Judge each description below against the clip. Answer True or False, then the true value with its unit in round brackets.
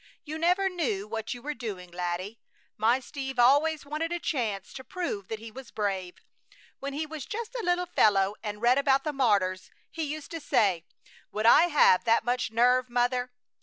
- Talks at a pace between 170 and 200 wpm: True (190 wpm)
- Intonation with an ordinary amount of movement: False (6.2 semitones)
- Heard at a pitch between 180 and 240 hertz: False (250 Hz)